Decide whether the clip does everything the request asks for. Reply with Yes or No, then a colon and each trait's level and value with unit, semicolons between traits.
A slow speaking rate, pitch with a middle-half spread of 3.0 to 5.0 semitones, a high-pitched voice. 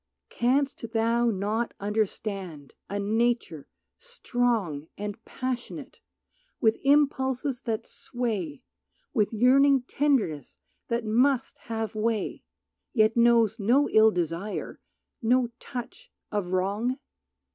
Yes: slow, 100 wpm; average, 3.4 semitones; high, 230 Hz